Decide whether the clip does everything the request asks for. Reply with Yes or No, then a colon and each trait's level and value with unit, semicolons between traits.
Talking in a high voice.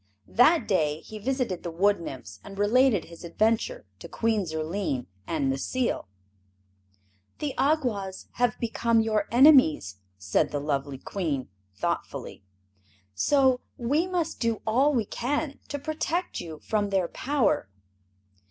Yes: high, 215 Hz